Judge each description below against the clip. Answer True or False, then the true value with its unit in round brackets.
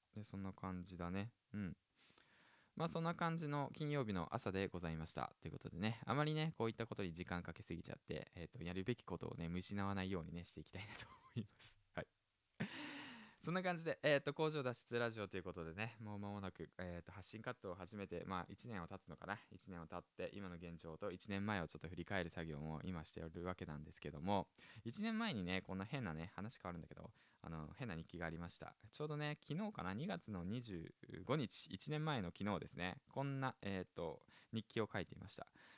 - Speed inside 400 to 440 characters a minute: True (410 characters per minute)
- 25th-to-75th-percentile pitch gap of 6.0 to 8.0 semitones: False (5.4 semitones)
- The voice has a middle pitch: False (100 Hz)